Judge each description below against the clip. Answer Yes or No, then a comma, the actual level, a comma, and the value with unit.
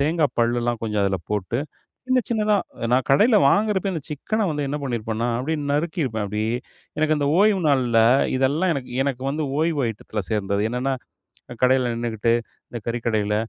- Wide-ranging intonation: Yes, wide, 5.7 semitones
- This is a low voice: Yes, low, 130 Hz